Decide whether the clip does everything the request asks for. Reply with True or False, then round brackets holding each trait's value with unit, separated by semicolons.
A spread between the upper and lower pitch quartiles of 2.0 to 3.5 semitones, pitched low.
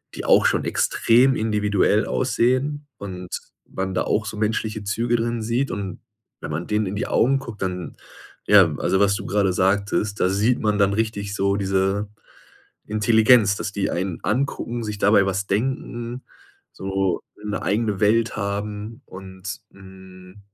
True (2.6 semitones; 105 Hz)